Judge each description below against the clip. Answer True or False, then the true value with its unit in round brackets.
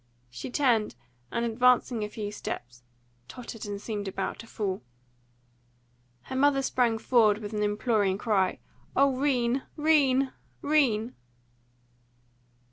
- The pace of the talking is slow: True (120 wpm)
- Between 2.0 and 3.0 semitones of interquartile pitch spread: False (3.8 semitones)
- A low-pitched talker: False (230 Hz)